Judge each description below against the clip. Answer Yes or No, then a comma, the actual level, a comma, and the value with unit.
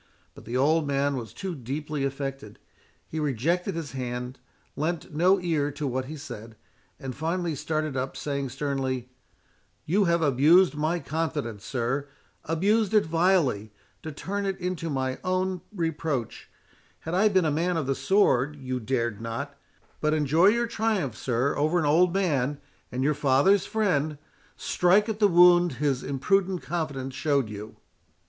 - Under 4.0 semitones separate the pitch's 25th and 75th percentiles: No, average, 4.7 semitones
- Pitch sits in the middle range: Yes, medium, 150 Hz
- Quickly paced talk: No, average, 150 wpm